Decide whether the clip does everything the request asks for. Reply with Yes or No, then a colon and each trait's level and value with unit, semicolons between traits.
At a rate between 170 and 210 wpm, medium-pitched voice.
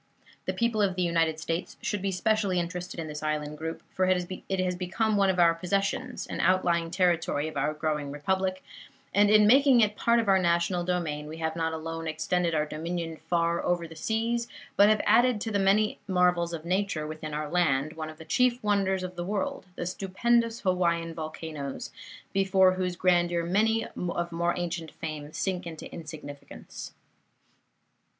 Yes: average, 180 wpm; medium, 175 Hz